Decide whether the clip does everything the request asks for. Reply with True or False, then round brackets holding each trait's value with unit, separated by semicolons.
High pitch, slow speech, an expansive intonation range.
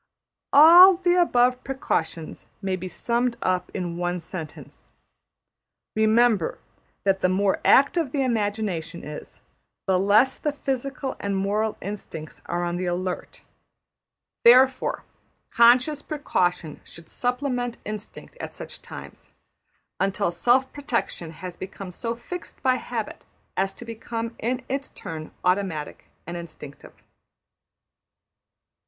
True (215 Hz; 120 wpm; 5.9 semitones)